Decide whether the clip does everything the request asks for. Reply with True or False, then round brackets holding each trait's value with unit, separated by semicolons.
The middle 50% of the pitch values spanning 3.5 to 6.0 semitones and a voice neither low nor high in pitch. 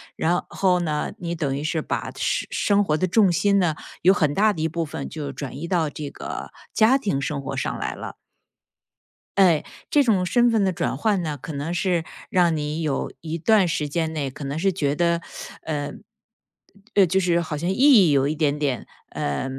True (4.2 semitones; 165 Hz)